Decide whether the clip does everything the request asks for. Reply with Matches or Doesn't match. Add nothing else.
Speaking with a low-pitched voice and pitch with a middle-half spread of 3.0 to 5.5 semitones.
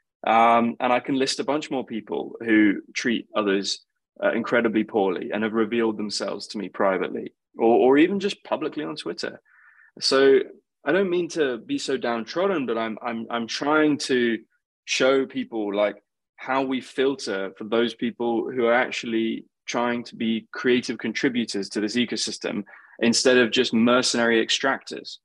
Doesn't match